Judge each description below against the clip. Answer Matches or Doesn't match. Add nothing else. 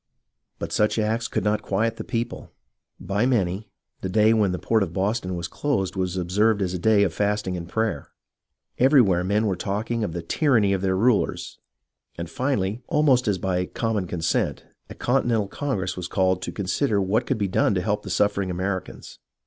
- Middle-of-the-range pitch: Doesn't match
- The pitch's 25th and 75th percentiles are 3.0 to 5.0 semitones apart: Matches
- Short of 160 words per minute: Doesn't match